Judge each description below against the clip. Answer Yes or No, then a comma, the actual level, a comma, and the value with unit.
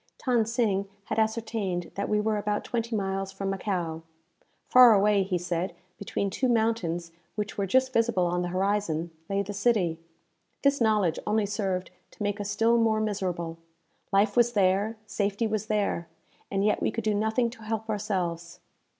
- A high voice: Yes, high, 205 Hz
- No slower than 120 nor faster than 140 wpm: No, average, 170 wpm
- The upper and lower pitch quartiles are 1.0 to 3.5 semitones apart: Yes, average, 2.7 semitones